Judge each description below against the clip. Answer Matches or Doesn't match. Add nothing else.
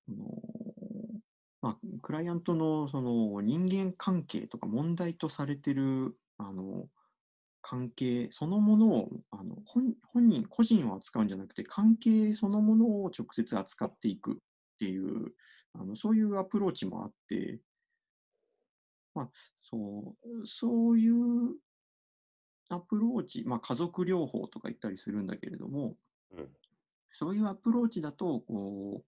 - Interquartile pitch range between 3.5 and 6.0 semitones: Doesn't match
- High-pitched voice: Matches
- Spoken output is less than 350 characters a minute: Matches